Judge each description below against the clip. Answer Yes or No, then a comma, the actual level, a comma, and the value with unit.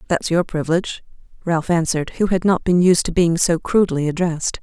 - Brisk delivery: No, average, 195 wpm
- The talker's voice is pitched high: No, medium, 170 Hz